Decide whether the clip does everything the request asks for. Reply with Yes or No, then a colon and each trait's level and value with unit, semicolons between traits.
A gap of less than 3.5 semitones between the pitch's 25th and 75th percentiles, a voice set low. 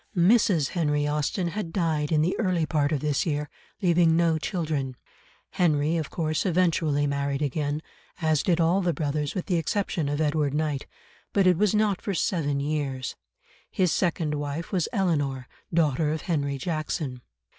No: average, 3.1 semitones; medium, 155 Hz